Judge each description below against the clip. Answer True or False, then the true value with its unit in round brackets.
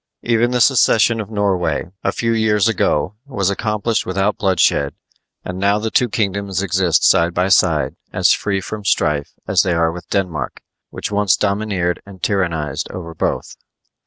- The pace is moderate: True (160 wpm)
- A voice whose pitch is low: True (95 Hz)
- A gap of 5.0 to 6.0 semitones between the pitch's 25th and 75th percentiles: False (3.3 semitones)